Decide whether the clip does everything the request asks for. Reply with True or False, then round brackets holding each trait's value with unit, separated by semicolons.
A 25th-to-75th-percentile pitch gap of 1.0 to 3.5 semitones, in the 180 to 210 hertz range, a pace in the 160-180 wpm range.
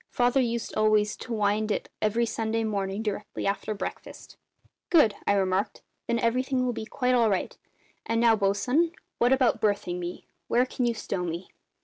False (3.0 semitones; 220 Hz; 170 wpm)